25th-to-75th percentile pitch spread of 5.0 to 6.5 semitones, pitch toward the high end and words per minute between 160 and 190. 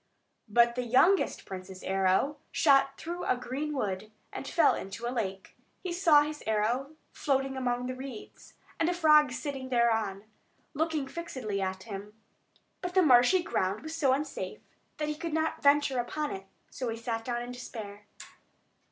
Yes: wide, 5.5 semitones; very high, 255 Hz; average, 165 wpm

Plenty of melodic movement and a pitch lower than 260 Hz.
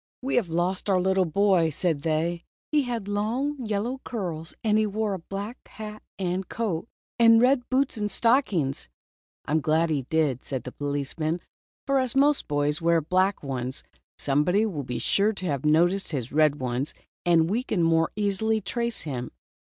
Yes: wide, 6.0 semitones; medium, 185 Hz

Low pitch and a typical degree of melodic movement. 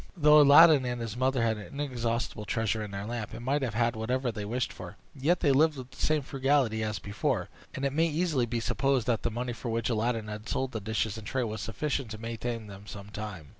Yes: low, 120 Hz; average, 3.7 semitones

